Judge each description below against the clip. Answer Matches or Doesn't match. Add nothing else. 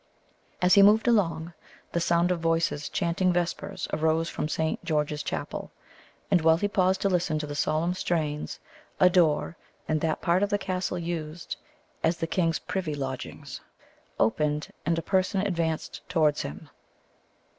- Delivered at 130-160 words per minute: Matches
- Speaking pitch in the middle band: Matches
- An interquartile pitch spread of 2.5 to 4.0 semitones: Matches